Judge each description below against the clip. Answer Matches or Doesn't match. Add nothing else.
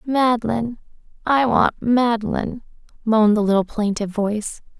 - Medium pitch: Doesn't match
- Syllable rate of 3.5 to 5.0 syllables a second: Matches